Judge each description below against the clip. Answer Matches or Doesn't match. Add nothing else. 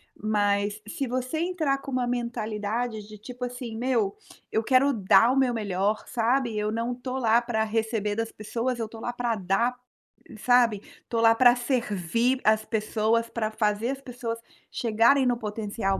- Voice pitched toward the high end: Matches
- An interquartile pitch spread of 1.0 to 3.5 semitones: Matches